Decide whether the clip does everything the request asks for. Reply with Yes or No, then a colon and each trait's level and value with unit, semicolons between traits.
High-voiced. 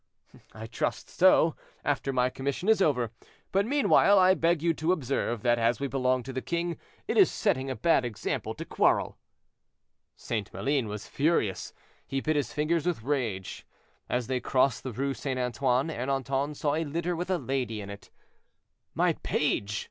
No: low, 135 Hz